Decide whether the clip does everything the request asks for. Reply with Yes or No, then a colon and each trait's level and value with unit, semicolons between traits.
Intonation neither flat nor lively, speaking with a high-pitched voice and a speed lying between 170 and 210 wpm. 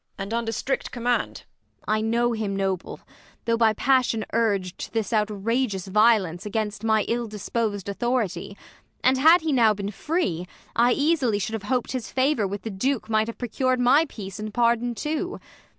Yes: average, 3.3 semitones; high, 225 Hz; average, 175 wpm